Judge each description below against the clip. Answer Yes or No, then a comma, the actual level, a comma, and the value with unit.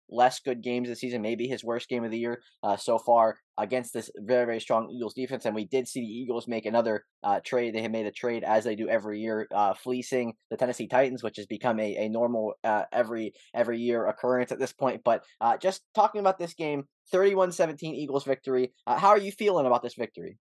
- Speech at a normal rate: No, fast, 230 wpm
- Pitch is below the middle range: Yes, low, 120 Hz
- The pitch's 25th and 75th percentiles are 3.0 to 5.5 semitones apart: No, narrow, 2.4 semitones